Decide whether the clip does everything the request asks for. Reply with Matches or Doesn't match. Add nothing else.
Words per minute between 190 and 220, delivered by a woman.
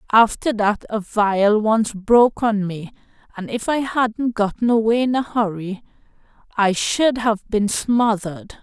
Doesn't match